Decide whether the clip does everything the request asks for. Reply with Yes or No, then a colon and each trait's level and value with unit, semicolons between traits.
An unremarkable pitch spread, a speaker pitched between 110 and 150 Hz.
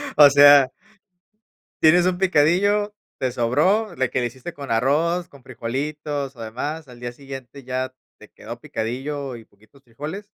Yes: average, 4.0 semitones; medium, 140 Hz